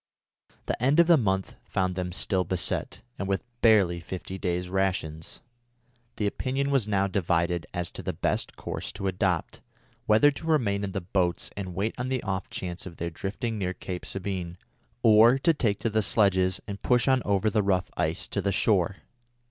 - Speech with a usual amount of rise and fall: Yes, average, 3.2 semitones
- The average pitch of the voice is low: Yes, very low, 95 Hz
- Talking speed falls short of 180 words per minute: No, average, 190 wpm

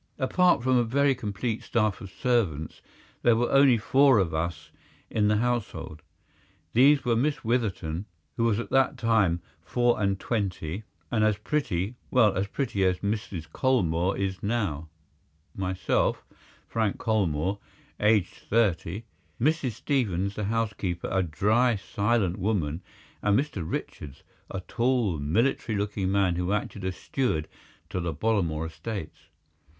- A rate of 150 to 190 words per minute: No, slow, 135 wpm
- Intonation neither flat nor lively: Yes, average, 4.8 semitones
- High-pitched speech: No, low, 105 Hz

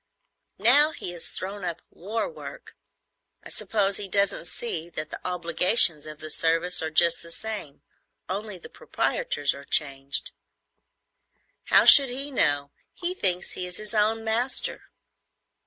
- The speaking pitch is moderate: Yes, medium, 180 Hz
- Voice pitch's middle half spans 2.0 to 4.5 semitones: No, average, 5.3 semitones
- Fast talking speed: No, average, 145 wpm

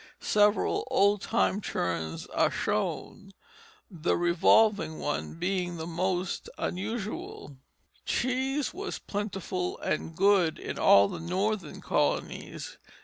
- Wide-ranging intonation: No, average, 3.8 semitones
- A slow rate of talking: Yes, slow, 105 wpm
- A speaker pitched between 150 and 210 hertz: Yes, high, 190 Hz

